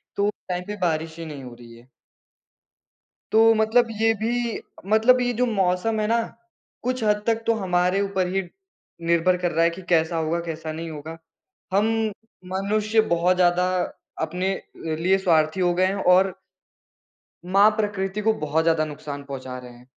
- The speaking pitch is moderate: Yes, medium, 180 Hz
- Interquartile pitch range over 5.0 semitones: No, average, 4.5 semitones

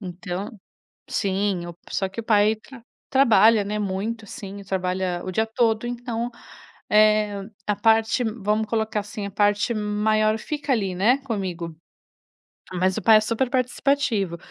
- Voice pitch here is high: Yes, high, 210 Hz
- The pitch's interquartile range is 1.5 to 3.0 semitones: Yes, narrow, 2.6 semitones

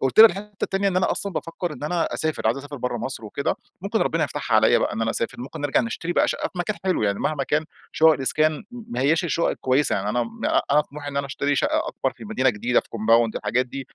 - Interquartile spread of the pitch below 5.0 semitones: No, average, 5.3 semitones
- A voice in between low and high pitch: Yes, medium, 145 Hz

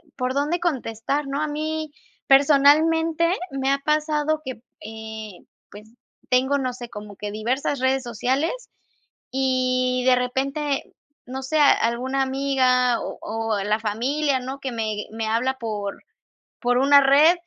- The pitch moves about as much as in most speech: Yes, average, 3.4 semitones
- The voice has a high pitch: Yes, very high, 265 Hz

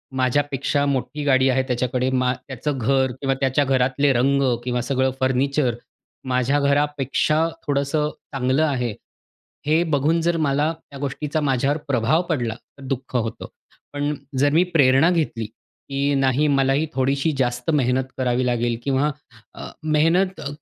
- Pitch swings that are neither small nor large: No, narrow, 2.3 semitones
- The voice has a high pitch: No, low, 135 Hz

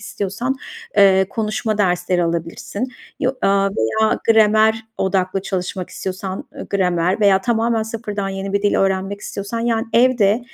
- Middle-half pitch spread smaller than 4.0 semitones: Yes, average, 2.7 semitones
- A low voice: No, high, 200 Hz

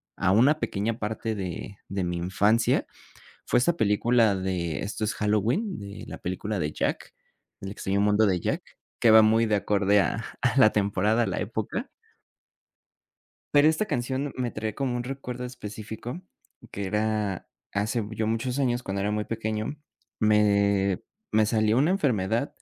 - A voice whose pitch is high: No, low, 110 Hz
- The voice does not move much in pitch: No, average, 3.2 semitones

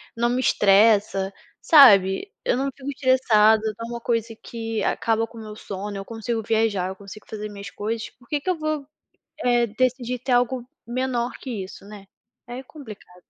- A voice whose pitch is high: Yes, high, 230 Hz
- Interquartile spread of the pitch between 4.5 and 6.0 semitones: No, average, 3.2 semitones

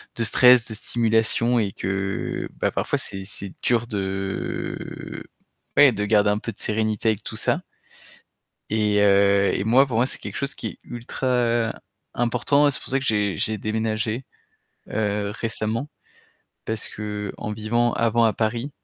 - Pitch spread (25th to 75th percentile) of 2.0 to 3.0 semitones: Yes, narrow, 2.4 semitones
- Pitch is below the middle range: Yes, low, 110 Hz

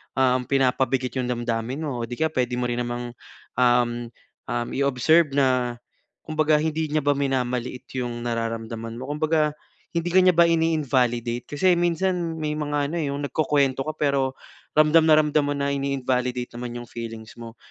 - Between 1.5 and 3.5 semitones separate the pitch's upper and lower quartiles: No, average, 4.0 semitones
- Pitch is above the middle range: No, low, 135 Hz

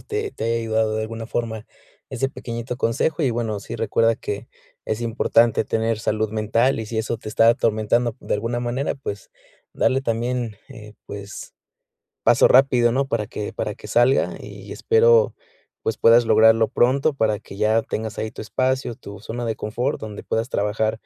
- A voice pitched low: Yes, low, 115 Hz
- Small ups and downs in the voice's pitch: Yes, narrow, 1.9 semitones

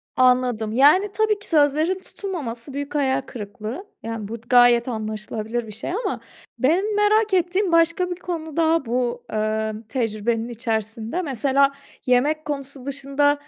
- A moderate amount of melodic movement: No, wide, 6.4 semitones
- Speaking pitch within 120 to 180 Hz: No, very high, 270 Hz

